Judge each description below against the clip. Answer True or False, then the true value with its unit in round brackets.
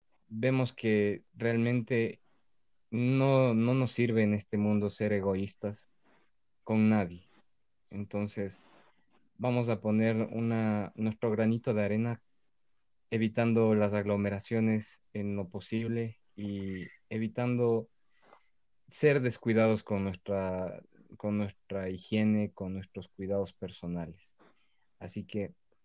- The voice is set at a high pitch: False (105 Hz)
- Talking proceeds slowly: True (100 wpm)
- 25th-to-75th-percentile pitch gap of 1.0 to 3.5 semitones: True (2.4 semitones)